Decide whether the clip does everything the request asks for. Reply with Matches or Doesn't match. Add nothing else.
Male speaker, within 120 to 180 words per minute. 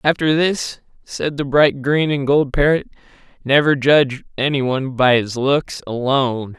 Matches